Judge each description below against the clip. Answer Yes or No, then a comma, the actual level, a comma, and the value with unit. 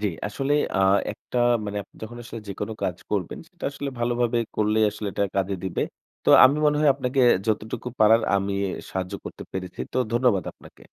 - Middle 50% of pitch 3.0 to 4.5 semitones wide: Yes, average, 3.7 semitones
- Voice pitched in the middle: No, low, 110 Hz